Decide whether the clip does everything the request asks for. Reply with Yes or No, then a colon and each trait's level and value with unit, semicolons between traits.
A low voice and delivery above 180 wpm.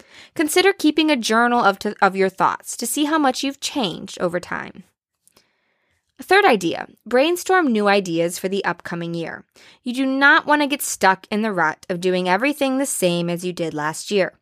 No: high, 220 Hz; average, 195 wpm